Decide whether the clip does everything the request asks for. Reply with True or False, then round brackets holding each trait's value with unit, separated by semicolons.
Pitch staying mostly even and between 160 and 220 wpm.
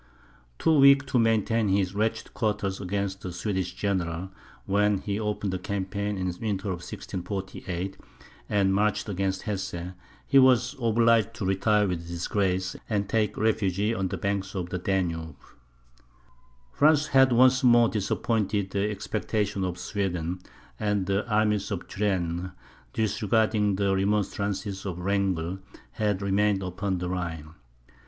False (2.3 semitones; 140 wpm)